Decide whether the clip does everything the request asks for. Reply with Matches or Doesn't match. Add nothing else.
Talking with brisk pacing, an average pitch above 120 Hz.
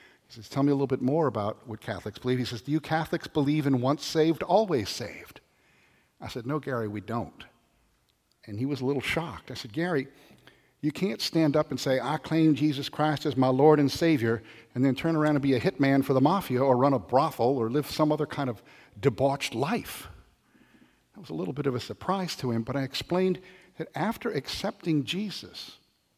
Matches